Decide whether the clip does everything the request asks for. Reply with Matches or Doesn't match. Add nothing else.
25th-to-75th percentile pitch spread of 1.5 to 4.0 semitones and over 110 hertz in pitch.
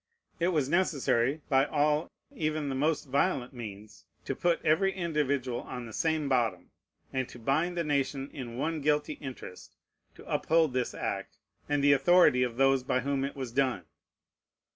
Matches